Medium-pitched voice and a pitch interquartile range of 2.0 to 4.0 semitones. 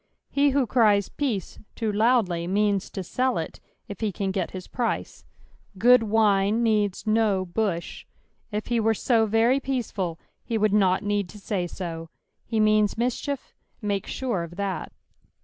No: high, 210 Hz; average, 3.0 semitones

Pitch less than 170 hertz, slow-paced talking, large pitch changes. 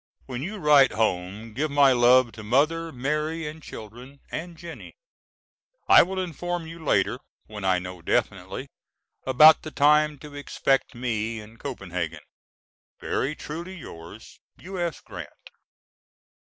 Yes: medium, 140 Hz; slow, 130 wpm; wide, 6.1 semitones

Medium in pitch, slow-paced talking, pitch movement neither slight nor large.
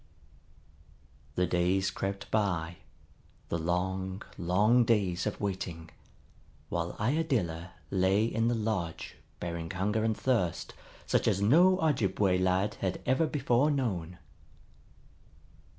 No: very low, 95 Hz; slow, 110 wpm; average, 4.2 semitones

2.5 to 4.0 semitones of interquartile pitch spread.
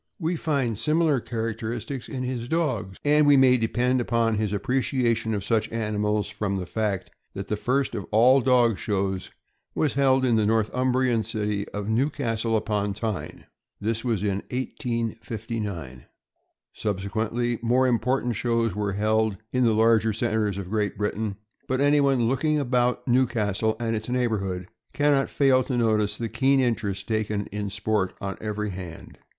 Yes: average, 3.3 semitones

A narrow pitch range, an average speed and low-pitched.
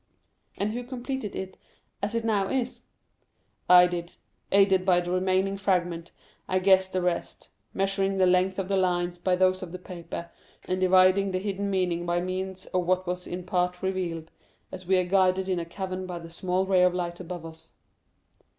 No: narrow, 1.3 semitones; average, 185 wpm; medium, 185 Hz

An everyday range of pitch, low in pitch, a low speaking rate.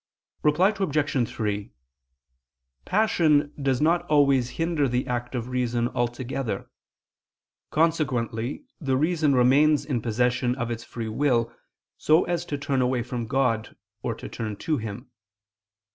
Yes: average, 3.9 semitones; low, 130 Hz; slow, 130 wpm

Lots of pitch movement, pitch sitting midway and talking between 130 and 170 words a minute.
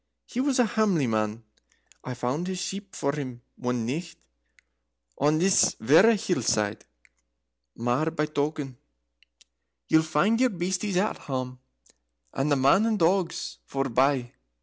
Yes: wide, 6.8 semitones; medium, 150 Hz; average, 140 wpm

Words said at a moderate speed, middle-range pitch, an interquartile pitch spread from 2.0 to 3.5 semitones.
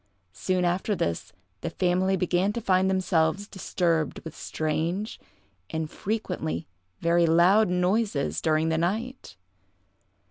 No: slow, 115 wpm; medium, 180 Hz; average, 3.1 semitones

